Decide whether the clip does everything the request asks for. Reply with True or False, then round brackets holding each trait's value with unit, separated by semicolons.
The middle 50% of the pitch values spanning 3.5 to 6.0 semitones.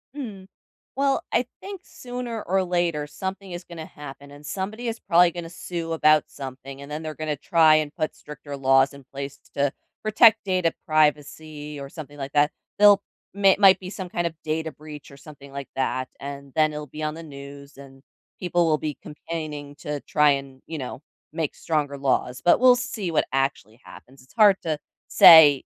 True (4.0 semitones)